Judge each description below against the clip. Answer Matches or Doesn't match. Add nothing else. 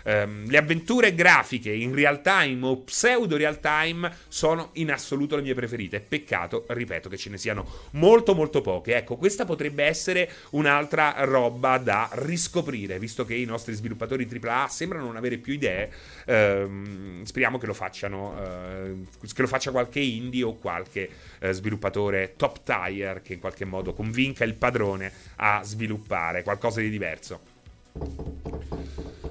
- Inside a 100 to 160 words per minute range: Matches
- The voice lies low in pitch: Matches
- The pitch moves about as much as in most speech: Doesn't match